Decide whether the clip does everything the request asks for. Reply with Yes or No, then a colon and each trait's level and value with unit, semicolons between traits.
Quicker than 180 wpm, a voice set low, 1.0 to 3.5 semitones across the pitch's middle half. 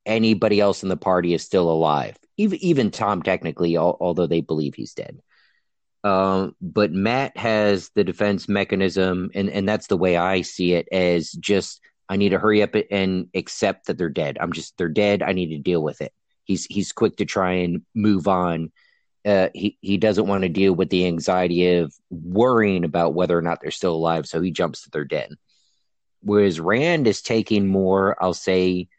Yes: average, 195 wpm; very low, 95 Hz; narrow, 2.6 semitones